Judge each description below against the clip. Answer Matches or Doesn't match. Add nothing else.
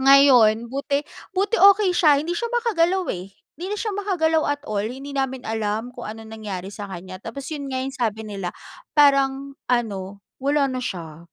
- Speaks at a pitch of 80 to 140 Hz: Doesn't match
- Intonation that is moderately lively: Doesn't match